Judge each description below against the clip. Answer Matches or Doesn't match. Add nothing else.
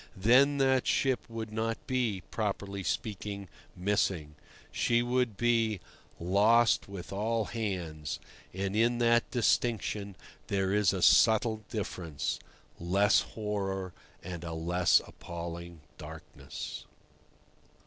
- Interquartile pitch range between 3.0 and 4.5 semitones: Matches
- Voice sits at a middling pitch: Doesn't match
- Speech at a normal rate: Doesn't match